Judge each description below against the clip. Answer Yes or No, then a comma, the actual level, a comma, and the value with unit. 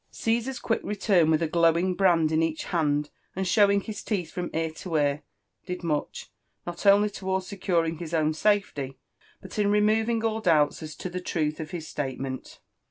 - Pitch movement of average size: Yes, average, 4.2 semitones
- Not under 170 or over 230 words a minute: Yes, average, 185 wpm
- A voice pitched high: No, medium, 175 Hz